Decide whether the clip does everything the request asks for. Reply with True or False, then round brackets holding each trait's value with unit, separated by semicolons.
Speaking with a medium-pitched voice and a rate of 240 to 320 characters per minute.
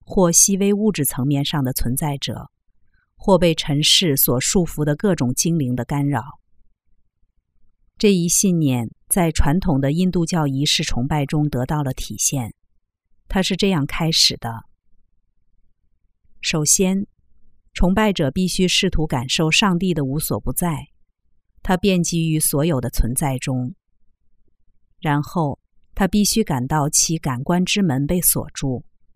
False (145 Hz; 200 characters per minute)